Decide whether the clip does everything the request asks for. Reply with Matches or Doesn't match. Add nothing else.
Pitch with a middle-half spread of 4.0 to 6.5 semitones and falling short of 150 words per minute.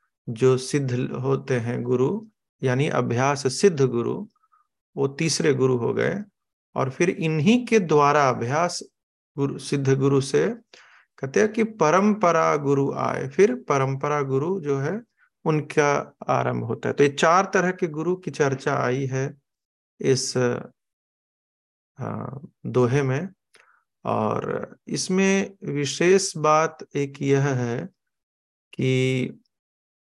Matches